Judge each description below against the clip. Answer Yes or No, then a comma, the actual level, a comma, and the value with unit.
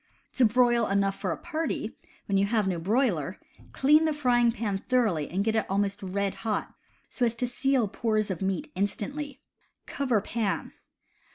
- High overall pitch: Yes, high, 220 Hz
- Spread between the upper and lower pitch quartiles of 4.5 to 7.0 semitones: No, average, 4.1 semitones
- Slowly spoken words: No, average, 170 wpm